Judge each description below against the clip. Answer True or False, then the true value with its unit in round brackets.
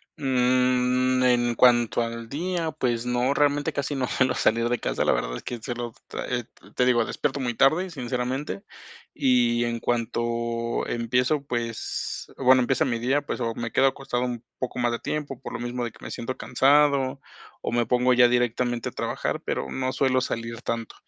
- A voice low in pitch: True (125 Hz)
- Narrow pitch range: True (1.9 semitones)